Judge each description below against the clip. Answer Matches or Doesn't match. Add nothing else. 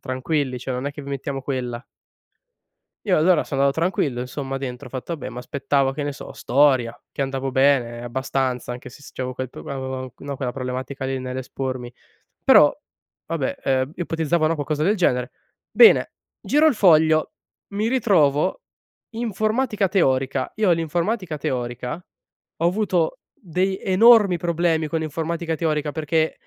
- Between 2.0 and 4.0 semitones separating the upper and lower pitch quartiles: Doesn't match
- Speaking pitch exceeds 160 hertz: Doesn't match